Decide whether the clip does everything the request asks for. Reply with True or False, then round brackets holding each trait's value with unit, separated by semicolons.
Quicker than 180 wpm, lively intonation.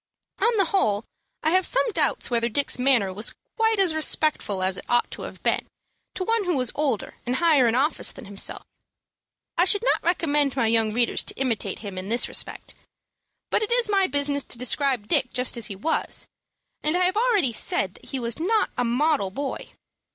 True (205 wpm; 7.4 semitones)